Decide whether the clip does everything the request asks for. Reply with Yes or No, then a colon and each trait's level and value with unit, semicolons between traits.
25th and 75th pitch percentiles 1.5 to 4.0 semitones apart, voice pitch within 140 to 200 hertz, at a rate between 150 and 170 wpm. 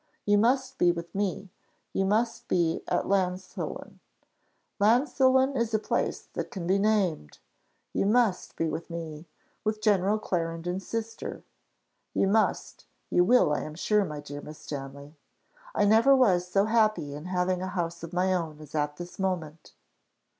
No: average, 4.4 semitones; medium, 185 Hz; average, 160 wpm